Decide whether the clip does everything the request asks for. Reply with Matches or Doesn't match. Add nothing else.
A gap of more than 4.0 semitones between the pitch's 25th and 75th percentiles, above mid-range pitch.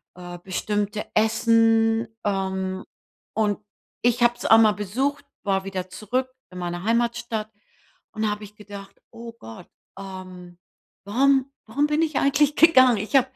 Doesn't match